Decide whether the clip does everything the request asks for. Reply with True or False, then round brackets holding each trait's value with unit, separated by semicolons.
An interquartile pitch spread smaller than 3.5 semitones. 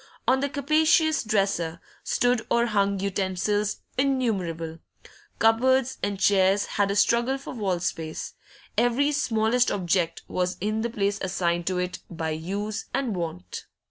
False (5.1 semitones)